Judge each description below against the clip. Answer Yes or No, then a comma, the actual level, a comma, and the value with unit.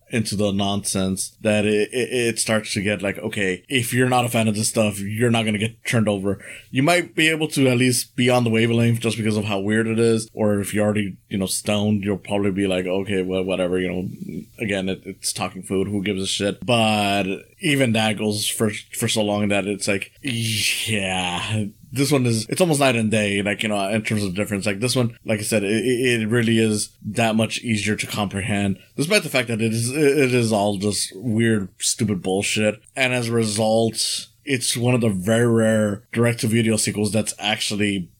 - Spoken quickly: Yes, fast, 220 wpm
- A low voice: Yes, low, 110 Hz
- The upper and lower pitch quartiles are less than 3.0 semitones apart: Yes, narrow, 2.4 semitones